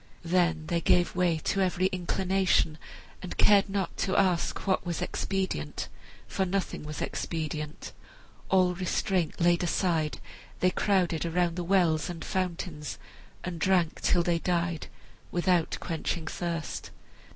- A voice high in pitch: No, medium, 175 Hz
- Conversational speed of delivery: No, slow, 130 wpm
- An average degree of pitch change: No, narrow, 2.1 semitones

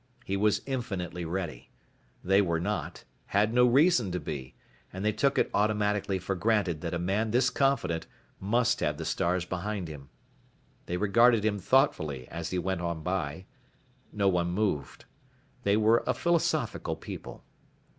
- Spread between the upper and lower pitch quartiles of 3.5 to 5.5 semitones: Yes, average, 4.0 semitones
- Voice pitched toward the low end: Yes, very low, 95 Hz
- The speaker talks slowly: No, average, 155 wpm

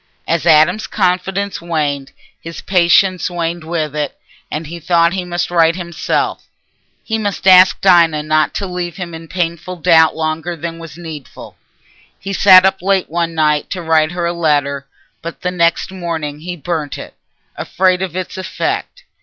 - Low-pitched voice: No, medium, 170 Hz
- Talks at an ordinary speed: Yes, average, 165 wpm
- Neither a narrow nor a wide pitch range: No, narrow, 2.3 semitones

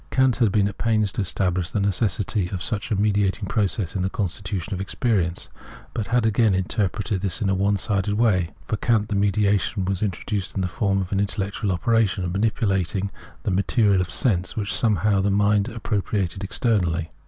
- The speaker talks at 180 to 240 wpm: Yes, average, 190 wpm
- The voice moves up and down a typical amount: No, narrow, 2.1 semitones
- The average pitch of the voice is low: Yes, low, 100 Hz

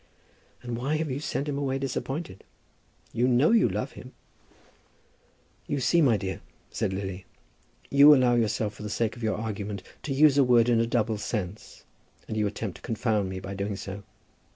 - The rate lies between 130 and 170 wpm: No, average, 185 wpm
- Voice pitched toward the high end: No, low, 115 Hz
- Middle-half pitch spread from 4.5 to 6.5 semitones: Yes, average, 4.8 semitones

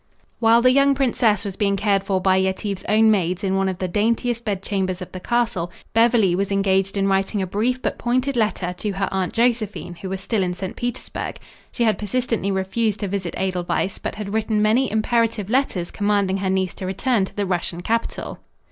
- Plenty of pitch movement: No, average, 3.2 semitones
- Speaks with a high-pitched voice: Yes, high, 200 Hz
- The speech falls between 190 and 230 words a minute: Yes, average, 200 wpm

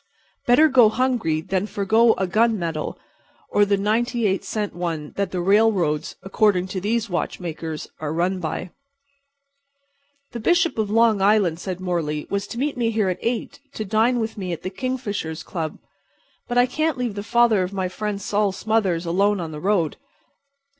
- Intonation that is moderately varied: Yes, average, 4.2 semitones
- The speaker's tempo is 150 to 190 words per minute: Yes, average, 165 wpm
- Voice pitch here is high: Yes, high, 200 Hz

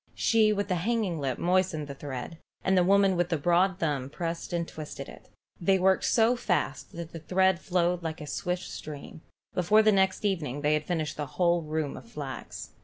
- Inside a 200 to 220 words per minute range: Yes, fast, 205 wpm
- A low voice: No, medium, 175 Hz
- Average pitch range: Yes, average, 3.8 semitones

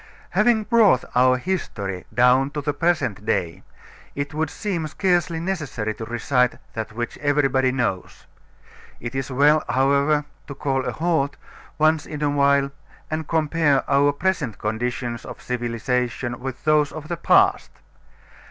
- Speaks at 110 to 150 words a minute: Yes, average, 145 wpm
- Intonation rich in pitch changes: No, average, 4.0 semitones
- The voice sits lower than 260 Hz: Yes, medium, 140 Hz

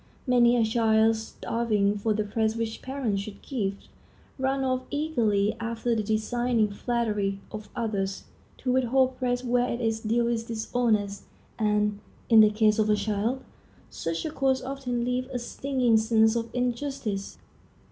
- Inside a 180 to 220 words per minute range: No, average, 155 wpm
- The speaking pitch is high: Yes, high, 230 Hz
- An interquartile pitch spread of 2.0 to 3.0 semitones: Yes, average, 2.7 semitones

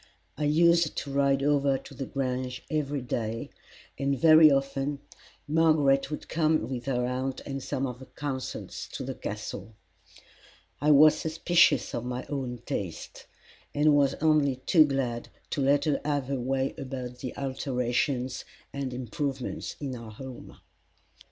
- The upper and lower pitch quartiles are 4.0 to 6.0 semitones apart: No, narrow, 2.5 semitones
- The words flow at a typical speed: Yes, average, 150 wpm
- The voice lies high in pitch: No, low, 135 Hz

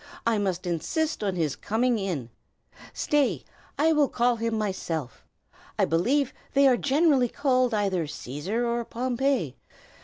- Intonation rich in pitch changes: Yes, wide, 6.6 semitones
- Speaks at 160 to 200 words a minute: No, average, 140 wpm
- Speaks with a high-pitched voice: Yes, high, 230 Hz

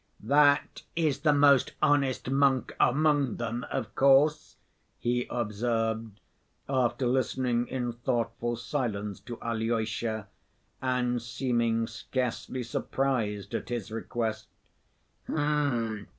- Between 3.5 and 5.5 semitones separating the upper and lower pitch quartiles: No, average, 2.8 semitones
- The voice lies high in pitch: No, low, 120 Hz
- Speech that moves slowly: Yes, slow, 95 wpm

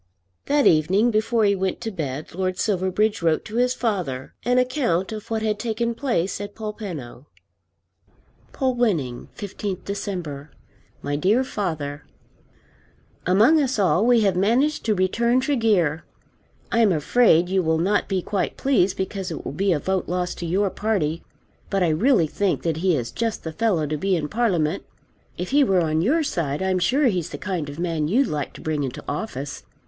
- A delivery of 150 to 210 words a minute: Yes, average, 180 wpm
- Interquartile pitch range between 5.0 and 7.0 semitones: Yes, wide, 5.4 semitones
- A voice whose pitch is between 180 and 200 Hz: Yes, high, 190 Hz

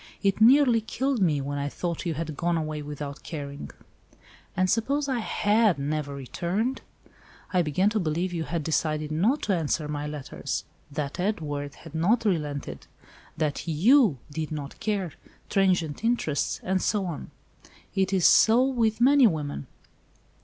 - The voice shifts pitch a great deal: Yes, wide, 6.2 semitones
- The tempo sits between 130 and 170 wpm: Yes, average, 150 wpm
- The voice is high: No, medium, 170 Hz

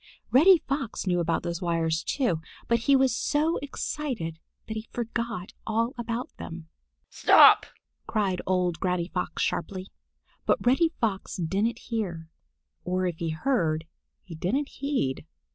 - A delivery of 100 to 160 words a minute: Yes, average, 140 wpm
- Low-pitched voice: No, high, 195 Hz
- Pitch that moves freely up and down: Yes, wide, 6.2 semitones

